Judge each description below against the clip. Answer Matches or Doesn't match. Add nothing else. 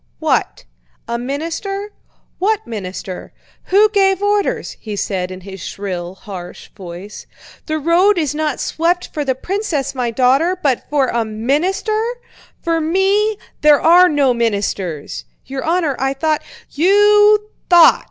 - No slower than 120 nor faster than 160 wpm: Matches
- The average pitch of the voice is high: Matches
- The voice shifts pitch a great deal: Matches